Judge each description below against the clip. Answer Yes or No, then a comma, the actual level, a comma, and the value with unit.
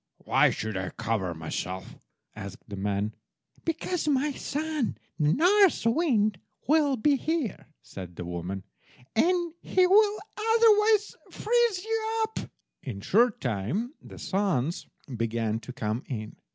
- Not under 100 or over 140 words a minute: Yes, slow, 135 wpm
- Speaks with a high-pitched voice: Yes, high, 230 Hz